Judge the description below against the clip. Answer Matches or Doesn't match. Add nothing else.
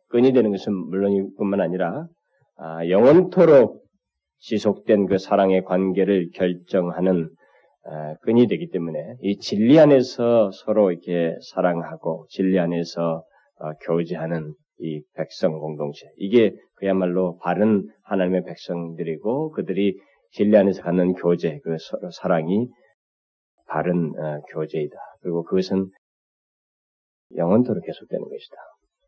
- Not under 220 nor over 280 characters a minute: Matches